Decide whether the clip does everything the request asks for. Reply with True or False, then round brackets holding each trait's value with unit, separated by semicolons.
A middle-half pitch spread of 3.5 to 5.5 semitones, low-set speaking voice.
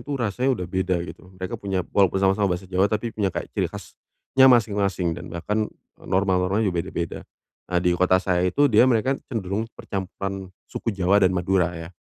False (2.5 semitones; 95 Hz)